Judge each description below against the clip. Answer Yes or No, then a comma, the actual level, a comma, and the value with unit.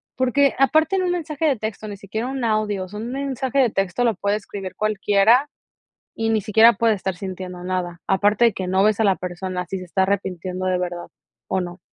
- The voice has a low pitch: No, high, 205 Hz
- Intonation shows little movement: No, average, 4.1 semitones